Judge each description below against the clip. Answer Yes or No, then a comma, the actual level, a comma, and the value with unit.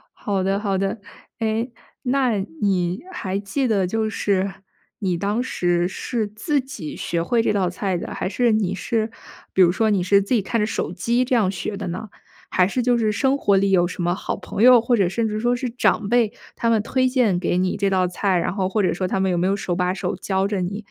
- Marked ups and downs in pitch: No, average, 3.5 semitones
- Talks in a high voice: Yes, high, 200 Hz